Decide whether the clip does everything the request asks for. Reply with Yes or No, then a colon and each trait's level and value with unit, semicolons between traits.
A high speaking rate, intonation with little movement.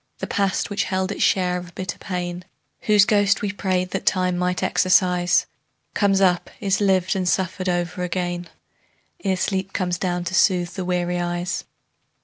No: average, 165 wpm; narrow, 1.4 semitones